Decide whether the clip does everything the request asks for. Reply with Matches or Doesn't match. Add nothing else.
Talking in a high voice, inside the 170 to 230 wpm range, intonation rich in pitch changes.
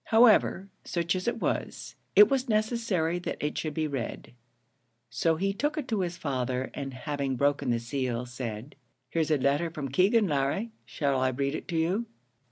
Doesn't match